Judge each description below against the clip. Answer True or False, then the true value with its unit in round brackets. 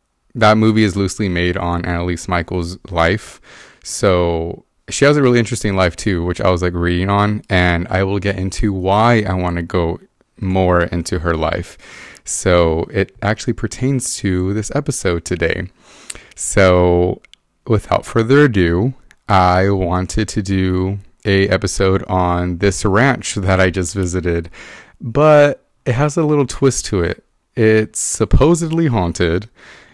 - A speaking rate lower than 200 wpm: True (145 wpm)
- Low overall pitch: True (95 Hz)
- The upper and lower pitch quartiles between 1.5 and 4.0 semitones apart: True (3.7 semitones)